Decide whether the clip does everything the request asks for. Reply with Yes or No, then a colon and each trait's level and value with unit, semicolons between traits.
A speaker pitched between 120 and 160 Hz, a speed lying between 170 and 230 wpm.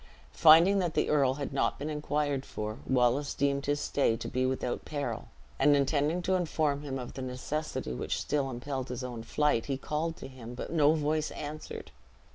Yes: medium, 140 Hz; average, 190 wpm